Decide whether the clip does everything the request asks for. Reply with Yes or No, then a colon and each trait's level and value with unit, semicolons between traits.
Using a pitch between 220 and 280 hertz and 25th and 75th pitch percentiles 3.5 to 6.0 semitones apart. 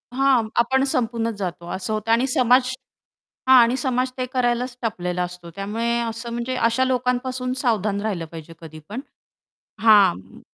Yes: high, 235 Hz; average, 4.1 semitones